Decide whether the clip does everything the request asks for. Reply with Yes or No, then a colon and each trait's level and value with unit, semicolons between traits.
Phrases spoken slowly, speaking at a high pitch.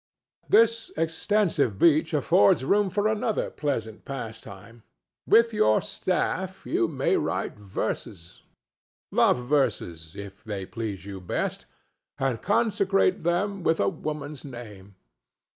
No: slow, 110 wpm; low, 135 Hz